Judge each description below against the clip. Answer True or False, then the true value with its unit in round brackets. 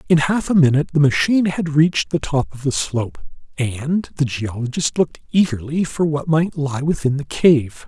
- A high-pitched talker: False (150 Hz)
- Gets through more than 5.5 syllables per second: False (5.2 syllables/s)